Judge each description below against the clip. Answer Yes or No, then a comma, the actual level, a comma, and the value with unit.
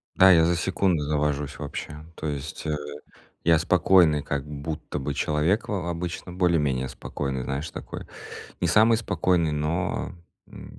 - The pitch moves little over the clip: No, average, 3.2 semitones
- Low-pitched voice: Yes, very low, 80 Hz